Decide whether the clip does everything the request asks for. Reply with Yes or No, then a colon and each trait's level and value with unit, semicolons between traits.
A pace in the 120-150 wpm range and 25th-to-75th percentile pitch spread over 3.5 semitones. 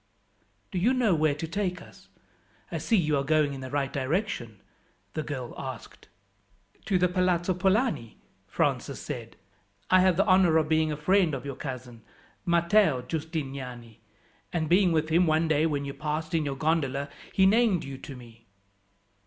No: average, 170 wpm; average, 4.7 semitones